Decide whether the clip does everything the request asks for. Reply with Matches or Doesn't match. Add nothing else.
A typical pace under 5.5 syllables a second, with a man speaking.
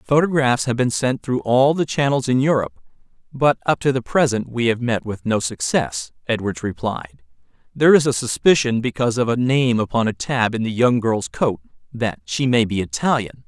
Matches